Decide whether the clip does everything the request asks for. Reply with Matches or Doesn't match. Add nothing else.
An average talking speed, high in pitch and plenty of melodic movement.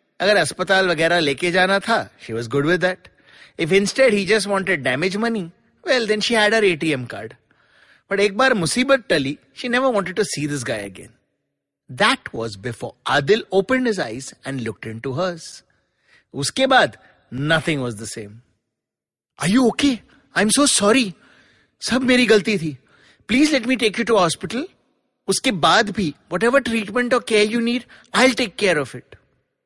Matches